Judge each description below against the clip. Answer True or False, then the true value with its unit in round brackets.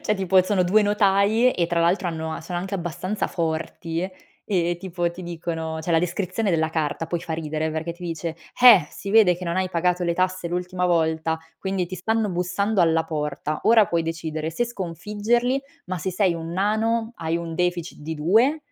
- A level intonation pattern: False (3.0 semitones)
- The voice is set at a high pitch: False (175 Hz)